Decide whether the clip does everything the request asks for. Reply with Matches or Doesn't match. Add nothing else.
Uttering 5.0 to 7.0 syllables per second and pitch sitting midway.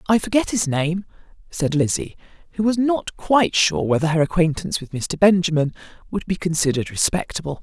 Matches